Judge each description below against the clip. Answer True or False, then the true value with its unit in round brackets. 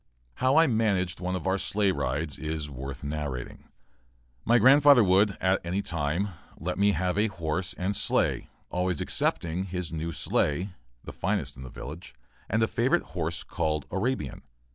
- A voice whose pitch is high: False (90 Hz)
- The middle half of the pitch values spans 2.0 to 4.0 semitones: False (4.6 semitones)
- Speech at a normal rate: True (165 wpm)